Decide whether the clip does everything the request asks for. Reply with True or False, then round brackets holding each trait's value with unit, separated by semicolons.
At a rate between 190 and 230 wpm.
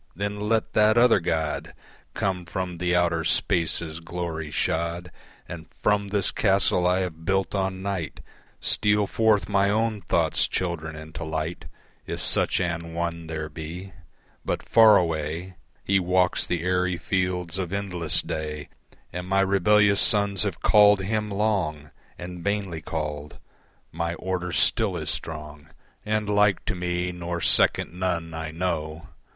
False (145 wpm)